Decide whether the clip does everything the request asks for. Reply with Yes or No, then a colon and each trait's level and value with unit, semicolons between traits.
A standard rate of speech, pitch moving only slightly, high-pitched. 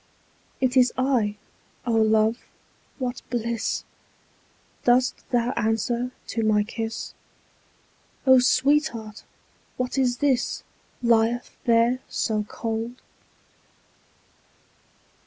No: slow, 85 wpm; narrow, 2.1 semitones; high, 235 Hz